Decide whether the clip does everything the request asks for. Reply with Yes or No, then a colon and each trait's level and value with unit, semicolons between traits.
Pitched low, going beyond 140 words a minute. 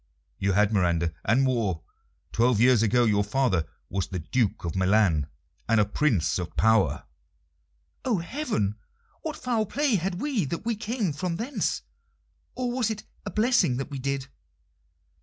Yes: low, 125 Hz; average, 160 wpm